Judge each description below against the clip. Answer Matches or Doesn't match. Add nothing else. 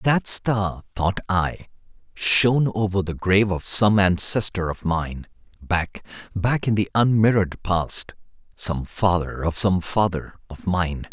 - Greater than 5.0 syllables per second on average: Doesn't match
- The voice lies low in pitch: Matches